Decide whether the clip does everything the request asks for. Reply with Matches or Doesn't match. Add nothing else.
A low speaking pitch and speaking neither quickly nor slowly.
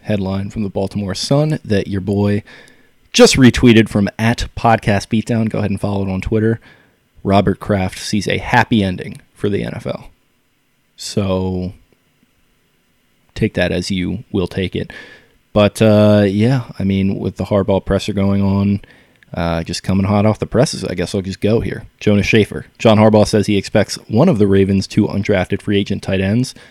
Matches